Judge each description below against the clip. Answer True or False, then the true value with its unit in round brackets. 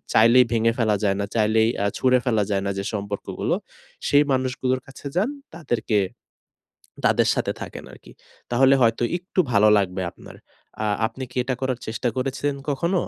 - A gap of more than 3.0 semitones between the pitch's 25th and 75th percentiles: True (3.6 semitones)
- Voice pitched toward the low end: True (120 Hz)